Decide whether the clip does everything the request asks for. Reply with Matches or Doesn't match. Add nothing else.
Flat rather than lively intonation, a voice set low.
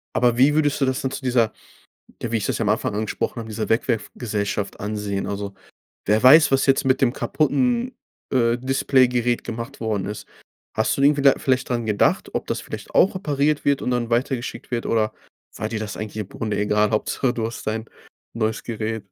Doesn't match